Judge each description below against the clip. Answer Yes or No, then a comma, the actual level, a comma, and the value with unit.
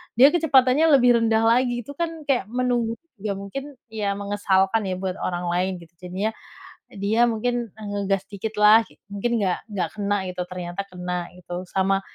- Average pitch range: Yes, average, 4.2 semitones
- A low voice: No, high, 205 Hz